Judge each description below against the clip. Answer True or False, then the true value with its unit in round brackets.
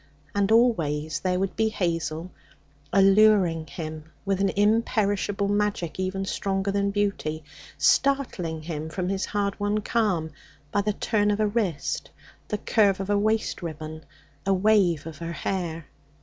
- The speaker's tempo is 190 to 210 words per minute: False (150 wpm)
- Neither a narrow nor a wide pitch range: True (3.8 semitones)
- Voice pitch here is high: True (195 Hz)